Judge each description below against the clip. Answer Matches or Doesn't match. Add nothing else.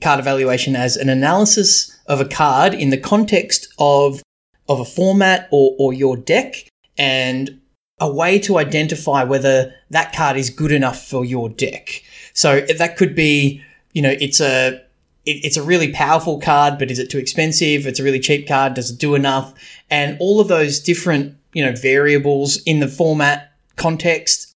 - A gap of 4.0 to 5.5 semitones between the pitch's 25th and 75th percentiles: Doesn't match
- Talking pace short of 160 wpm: Doesn't match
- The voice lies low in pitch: Doesn't match